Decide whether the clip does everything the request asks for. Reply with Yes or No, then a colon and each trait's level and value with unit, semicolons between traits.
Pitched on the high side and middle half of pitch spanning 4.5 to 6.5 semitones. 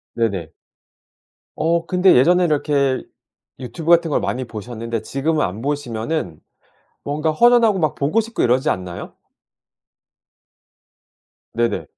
No: medium, 145 Hz; wide, 6.2 semitones